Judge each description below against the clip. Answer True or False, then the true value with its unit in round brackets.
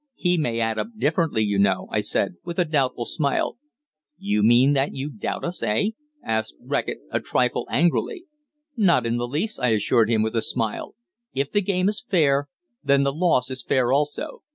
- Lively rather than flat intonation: True (6.3 semitones)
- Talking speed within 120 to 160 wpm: False (190 wpm)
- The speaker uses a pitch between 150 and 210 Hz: False (135 Hz)